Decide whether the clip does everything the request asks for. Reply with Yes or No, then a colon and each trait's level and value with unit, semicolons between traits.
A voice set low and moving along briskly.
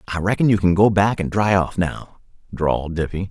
Yes: very low, 95 Hz; fast, 220 wpm